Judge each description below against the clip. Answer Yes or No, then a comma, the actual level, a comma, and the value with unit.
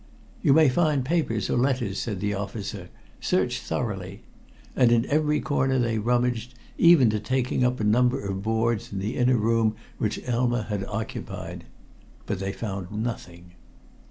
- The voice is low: Yes, low, 115 Hz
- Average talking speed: Yes, average, 155 wpm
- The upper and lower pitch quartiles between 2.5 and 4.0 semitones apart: Yes, average, 3.5 semitones